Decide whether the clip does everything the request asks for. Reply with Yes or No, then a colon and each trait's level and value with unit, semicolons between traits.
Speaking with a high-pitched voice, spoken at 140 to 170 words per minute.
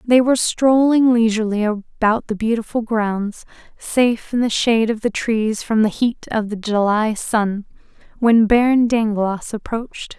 Yes: high, 225 Hz; average, 155 wpm